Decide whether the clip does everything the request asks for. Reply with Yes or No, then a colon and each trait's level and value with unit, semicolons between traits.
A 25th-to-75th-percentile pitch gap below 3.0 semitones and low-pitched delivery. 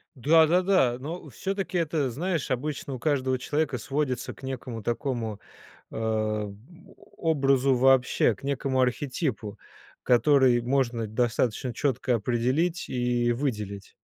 No: average, 3.6 semitones; low, 130 Hz